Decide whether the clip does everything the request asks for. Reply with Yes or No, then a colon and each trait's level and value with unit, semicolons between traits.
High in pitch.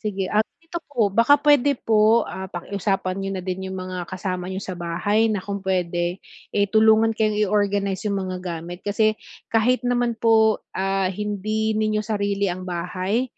Yes: high, 200 Hz